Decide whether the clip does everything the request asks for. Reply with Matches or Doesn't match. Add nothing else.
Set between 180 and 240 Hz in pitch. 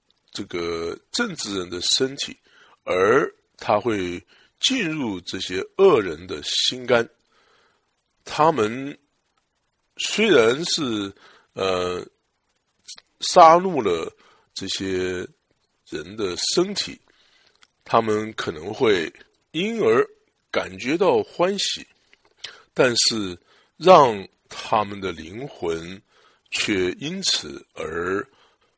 Matches